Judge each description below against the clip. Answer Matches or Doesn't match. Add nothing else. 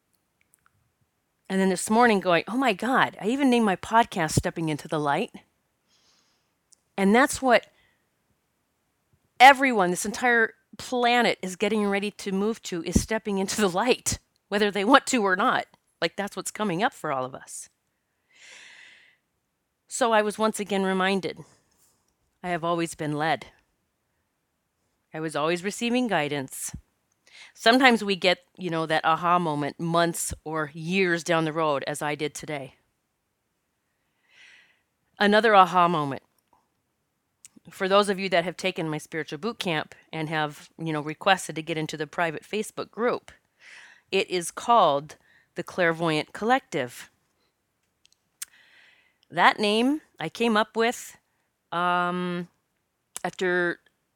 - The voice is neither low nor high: Matches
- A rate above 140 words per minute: Doesn't match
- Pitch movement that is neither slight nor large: Matches